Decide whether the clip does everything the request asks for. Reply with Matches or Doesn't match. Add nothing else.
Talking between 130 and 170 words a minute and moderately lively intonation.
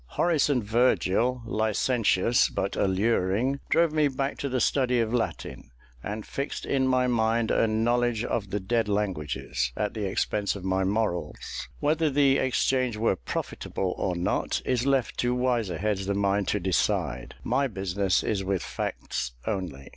Matches